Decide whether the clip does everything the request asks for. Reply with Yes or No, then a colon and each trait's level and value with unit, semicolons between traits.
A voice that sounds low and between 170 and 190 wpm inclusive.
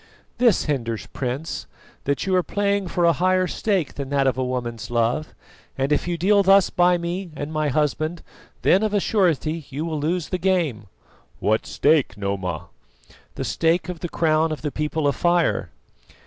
No: medium, 160 Hz; average, 180 wpm